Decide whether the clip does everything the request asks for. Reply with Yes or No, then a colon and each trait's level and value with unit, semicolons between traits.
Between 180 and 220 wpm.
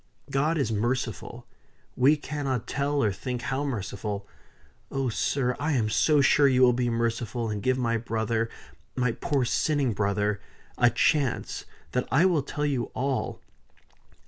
No: average, 150 wpm